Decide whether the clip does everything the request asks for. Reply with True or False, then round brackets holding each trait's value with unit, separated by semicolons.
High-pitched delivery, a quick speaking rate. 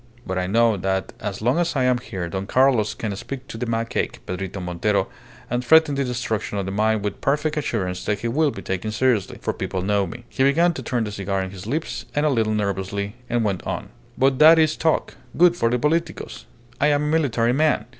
False (115 Hz; 225 wpm)